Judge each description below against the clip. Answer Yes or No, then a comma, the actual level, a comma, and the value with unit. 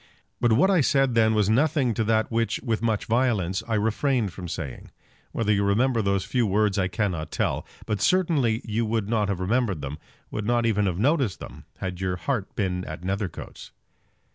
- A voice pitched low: Yes, low, 110 Hz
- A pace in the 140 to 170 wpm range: No, average, 190 wpm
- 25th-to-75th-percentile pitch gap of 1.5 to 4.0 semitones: Yes, average, 3.6 semitones